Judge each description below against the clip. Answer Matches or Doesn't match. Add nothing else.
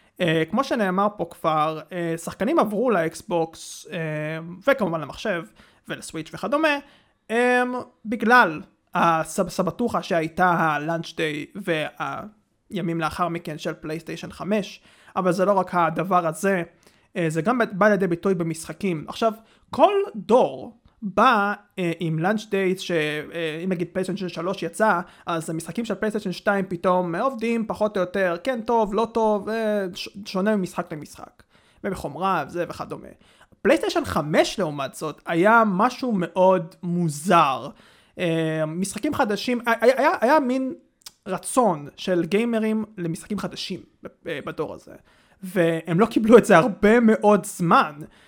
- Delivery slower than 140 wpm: Matches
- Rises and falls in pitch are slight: Doesn't match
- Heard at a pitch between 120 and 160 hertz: Doesn't match